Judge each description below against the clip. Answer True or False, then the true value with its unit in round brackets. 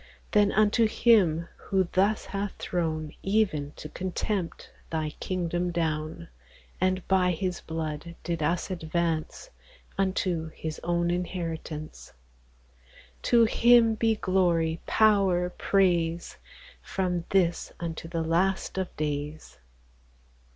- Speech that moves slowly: True (110 wpm)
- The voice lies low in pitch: False (175 Hz)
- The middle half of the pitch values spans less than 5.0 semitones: True (2.9 semitones)